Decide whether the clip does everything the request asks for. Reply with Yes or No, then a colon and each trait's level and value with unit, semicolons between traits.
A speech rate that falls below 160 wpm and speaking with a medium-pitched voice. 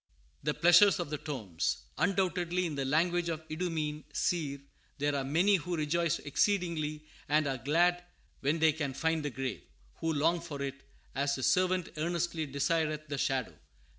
No: average, 165 wpm; medium, 155 Hz